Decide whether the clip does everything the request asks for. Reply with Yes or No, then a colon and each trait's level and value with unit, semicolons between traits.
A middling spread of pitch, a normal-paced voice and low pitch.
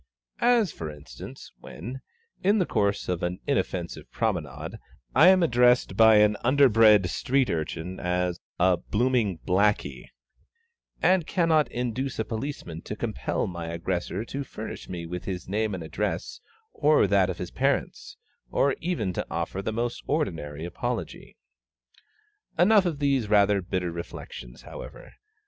No: wide, 7.2 semitones; average, 145 wpm; low, 105 Hz